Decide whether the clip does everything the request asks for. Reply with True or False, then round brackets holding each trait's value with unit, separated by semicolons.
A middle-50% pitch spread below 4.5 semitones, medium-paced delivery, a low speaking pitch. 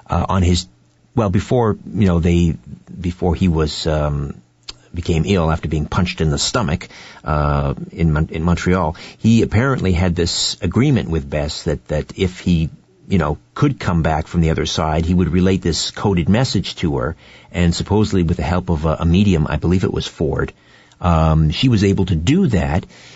True (2.8 semitones; 190 wpm; 85 Hz)